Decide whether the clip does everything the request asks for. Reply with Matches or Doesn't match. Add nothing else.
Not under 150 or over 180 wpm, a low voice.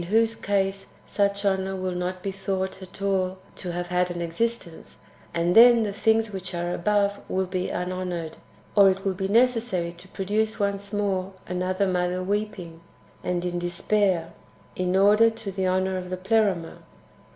Doesn't match